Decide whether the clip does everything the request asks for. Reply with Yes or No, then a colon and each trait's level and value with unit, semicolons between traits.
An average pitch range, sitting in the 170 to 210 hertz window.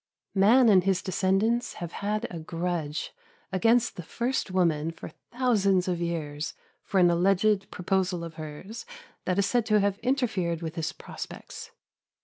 Yes: average, 3.8 semitones; medium, 185 Hz